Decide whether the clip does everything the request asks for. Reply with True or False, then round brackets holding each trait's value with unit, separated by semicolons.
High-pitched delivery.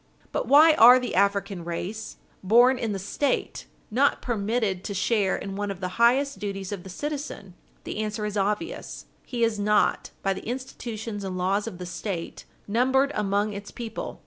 True (210 Hz)